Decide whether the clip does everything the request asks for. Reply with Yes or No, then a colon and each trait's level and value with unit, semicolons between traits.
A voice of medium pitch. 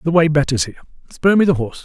Yes: medium, 155 Hz